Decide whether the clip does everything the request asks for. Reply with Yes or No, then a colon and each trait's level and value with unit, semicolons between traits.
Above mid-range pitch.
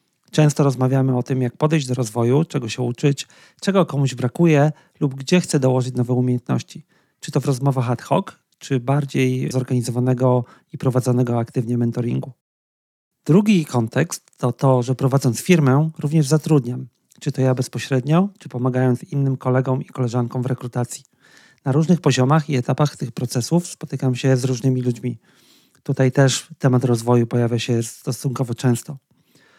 No: low, 130 Hz